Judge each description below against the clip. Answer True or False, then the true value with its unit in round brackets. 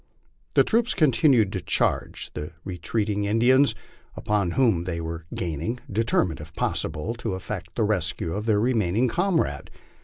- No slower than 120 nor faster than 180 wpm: True (150 wpm)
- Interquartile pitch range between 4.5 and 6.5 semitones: True (5.6 semitones)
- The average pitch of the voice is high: False (105 Hz)